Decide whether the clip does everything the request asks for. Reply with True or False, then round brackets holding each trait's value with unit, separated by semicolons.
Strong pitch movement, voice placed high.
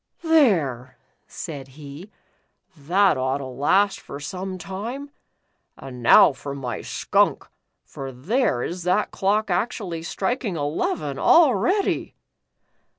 False (6.9 semitones; 175 Hz)